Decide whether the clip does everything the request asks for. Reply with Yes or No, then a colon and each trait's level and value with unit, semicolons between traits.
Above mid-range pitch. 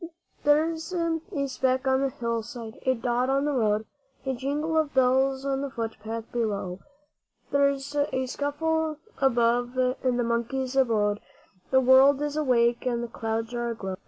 Yes: very high, 260 Hz